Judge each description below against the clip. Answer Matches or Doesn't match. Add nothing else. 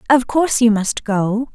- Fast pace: Doesn't match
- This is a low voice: Doesn't match